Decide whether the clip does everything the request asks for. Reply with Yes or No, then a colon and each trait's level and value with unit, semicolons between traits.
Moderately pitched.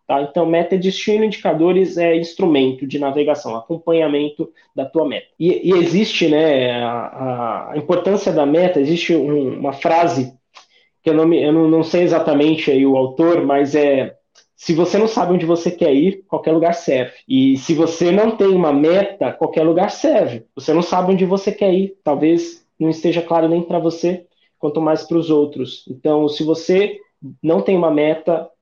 Yes: medium, 165 Hz